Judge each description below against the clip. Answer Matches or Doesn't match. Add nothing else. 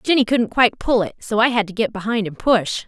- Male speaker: Doesn't match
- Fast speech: Matches